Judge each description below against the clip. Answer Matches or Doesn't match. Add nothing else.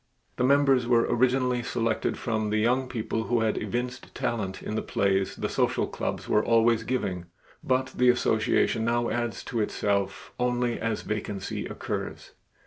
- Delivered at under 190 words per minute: Matches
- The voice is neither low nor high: Doesn't match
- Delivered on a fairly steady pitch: Matches